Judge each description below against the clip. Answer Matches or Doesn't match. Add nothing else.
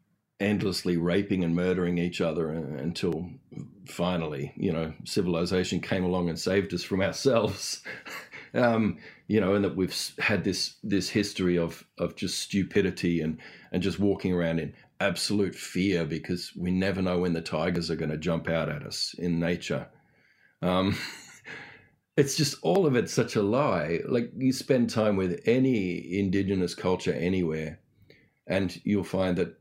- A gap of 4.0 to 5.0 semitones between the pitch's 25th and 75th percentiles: Doesn't match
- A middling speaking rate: Matches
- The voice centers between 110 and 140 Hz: Doesn't match